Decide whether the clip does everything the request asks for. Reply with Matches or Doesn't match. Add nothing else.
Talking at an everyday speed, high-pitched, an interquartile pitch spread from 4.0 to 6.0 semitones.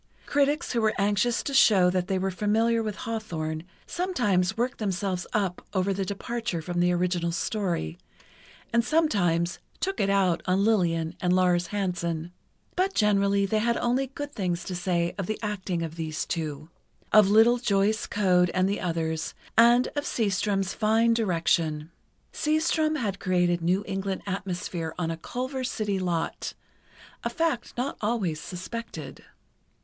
Matches